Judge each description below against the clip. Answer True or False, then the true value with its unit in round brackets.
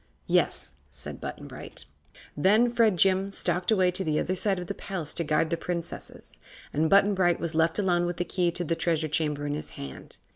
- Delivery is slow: False (205 wpm)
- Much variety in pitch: False (3.0 semitones)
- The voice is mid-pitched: True (175 Hz)